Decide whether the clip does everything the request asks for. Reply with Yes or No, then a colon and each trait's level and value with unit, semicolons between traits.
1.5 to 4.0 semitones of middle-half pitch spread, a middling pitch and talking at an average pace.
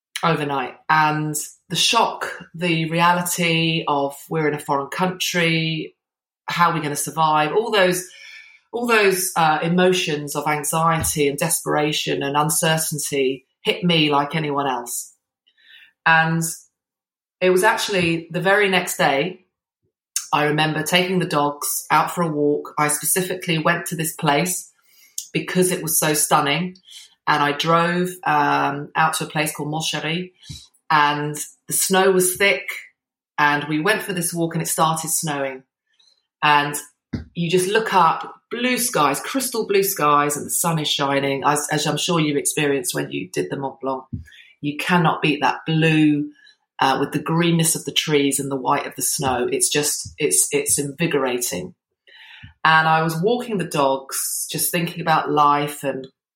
Yes: average, 3.5 semitones; medium, 160 Hz; average, 160 wpm